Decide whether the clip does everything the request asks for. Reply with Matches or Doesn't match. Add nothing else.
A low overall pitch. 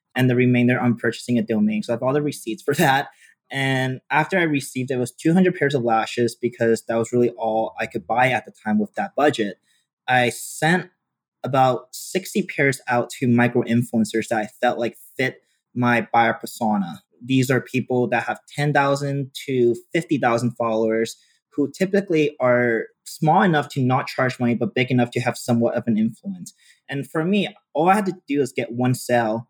Matches